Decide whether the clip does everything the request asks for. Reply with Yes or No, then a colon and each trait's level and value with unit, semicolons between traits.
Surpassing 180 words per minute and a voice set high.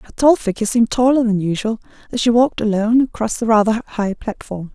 Yes: average, 200 wpm; high, 225 Hz